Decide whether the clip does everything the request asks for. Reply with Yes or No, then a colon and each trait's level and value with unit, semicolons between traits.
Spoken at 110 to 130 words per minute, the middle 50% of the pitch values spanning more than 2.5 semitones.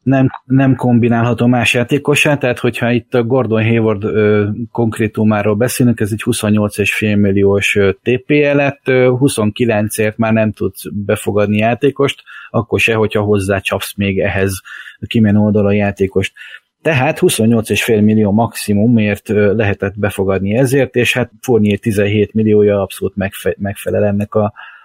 Yes: average, 125 wpm; average, 2.9 semitones